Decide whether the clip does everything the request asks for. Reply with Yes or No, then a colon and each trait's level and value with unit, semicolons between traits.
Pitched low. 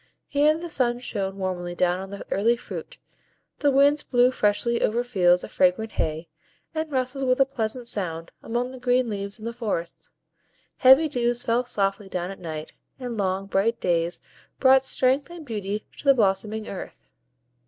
No: high, 230 Hz